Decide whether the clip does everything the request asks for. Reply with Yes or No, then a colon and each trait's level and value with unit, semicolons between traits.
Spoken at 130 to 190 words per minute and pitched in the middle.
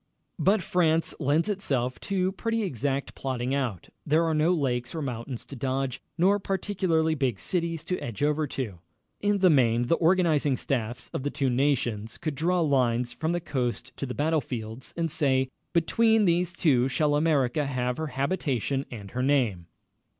Yes: average, 170 wpm; medium, 145 Hz